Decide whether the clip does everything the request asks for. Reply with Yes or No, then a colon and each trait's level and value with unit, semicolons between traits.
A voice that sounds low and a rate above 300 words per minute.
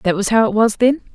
No: high, 220 Hz; fast, 315 wpm